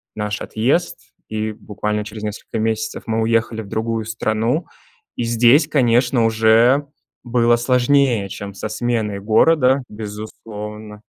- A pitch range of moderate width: No, narrow, 2.2 semitones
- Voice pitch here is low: Yes, low, 110 Hz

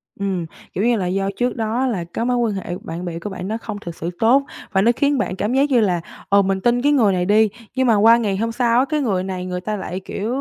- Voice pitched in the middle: No, high, 210 Hz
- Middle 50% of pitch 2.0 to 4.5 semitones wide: Yes, average, 4.2 semitones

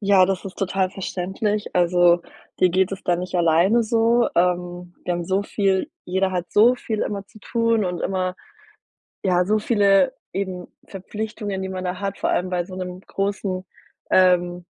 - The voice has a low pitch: No, high, 190 Hz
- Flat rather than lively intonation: Yes, narrow, 2.2 semitones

